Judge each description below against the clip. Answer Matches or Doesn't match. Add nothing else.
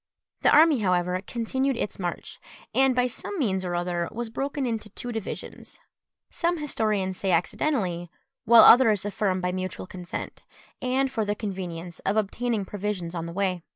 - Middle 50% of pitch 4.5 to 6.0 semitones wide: Matches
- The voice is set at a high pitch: Matches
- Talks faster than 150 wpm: Matches